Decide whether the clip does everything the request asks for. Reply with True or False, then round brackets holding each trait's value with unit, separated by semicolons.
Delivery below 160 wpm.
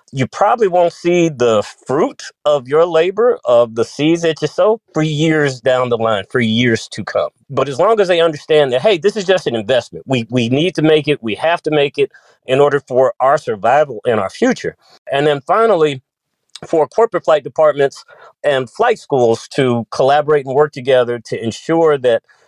False (200 wpm)